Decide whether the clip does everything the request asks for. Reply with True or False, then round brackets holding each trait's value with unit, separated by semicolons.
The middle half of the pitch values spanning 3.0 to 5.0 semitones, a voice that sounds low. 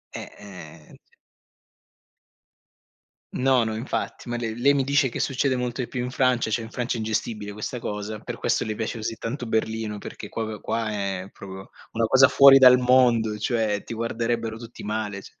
False (2.6 semitones; 115 Hz)